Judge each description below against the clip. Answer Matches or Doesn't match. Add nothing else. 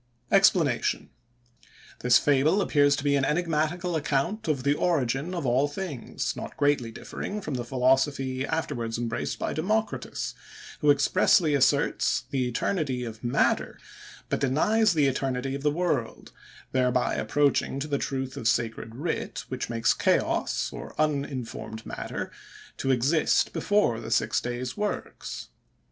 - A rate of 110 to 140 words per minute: Matches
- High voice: Doesn't match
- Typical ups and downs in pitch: Matches